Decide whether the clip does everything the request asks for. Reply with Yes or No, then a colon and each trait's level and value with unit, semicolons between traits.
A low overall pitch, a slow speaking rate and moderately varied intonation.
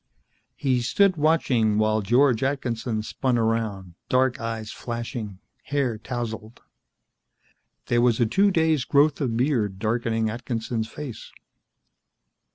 Yes: low, 120 Hz; slow, 115 wpm; average, 3.2 semitones